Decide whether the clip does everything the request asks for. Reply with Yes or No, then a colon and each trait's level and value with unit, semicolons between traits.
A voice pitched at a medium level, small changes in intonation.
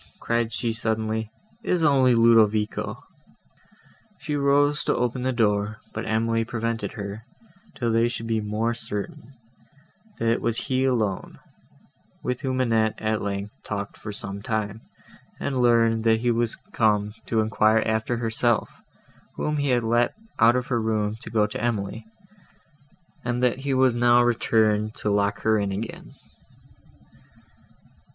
No: low, 115 Hz; narrow, 2.0 semitones